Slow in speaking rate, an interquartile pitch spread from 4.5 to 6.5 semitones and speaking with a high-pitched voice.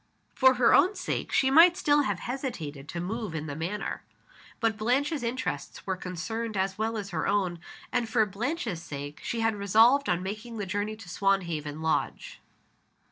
No: average, 175 wpm; wide, 5.4 semitones; high, 210 Hz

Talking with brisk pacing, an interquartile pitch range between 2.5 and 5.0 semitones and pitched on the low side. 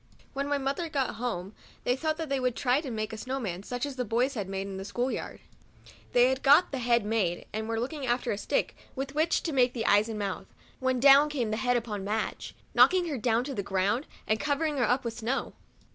No: fast, 260 wpm; average, 4.0 semitones; high, 245 Hz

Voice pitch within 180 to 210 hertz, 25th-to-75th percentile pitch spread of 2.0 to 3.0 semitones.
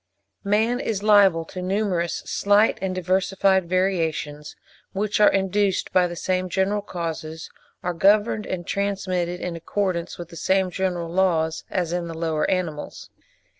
Yes: medium, 185 Hz; narrow, 2.6 semitones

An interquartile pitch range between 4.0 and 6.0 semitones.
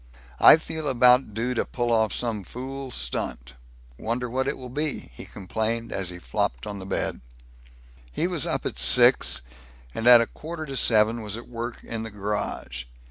No: average, 3.4 semitones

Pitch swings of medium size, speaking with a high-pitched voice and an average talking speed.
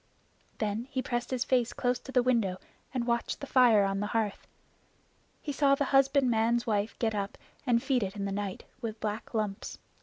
Yes: average, 3.5 semitones; high, 235 Hz; average, 190 wpm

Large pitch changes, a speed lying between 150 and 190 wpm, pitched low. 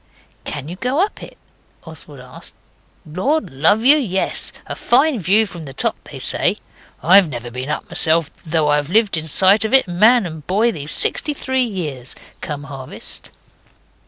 No: wide, 7.1 semitones; average, 170 wpm; medium, 175 Hz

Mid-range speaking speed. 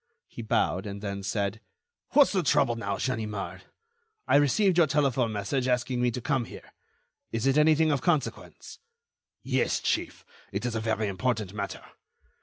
Yes: average, 160 wpm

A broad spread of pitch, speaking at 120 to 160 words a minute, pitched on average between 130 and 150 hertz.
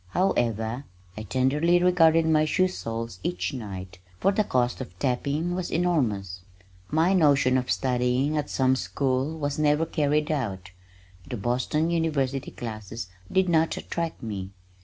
Yes: wide, 5.7 semitones; average, 140 wpm; low, 135 Hz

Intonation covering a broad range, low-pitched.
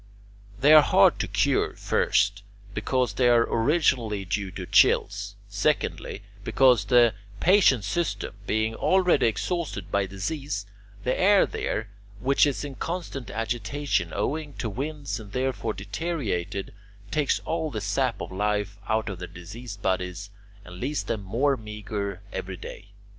Yes: wide, 5.7 semitones; low, 115 Hz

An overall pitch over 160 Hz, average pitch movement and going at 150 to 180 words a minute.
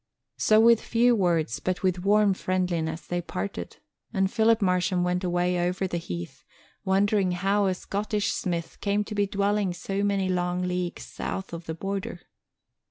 No: medium, 185 Hz; narrow, 2.3 semitones; average, 165 wpm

